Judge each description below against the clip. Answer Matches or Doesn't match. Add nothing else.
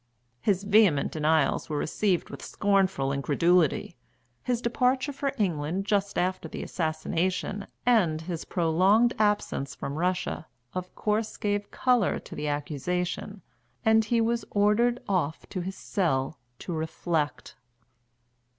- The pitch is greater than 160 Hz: Matches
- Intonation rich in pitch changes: Doesn't match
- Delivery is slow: Matches